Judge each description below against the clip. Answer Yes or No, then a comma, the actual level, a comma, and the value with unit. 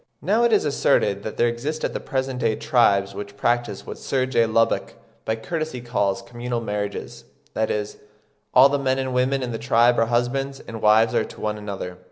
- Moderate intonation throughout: Yes, average, 3.6 semitones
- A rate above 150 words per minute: Yes, average, 200 wpm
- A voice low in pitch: Yes, low, 120 Hz